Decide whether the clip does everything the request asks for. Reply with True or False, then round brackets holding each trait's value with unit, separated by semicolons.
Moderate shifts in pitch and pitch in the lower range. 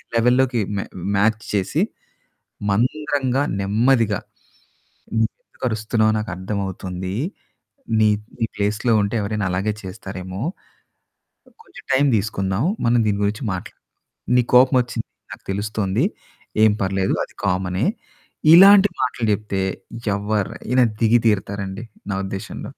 True (3.7 semitones; 105 Hz)